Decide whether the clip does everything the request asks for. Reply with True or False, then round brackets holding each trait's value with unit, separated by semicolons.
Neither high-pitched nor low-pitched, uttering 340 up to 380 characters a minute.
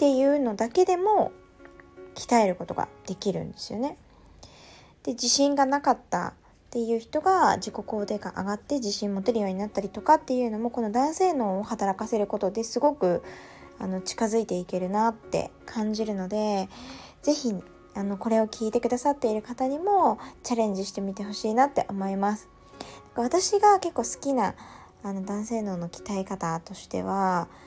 False (220 Hz; 350 characters per minute)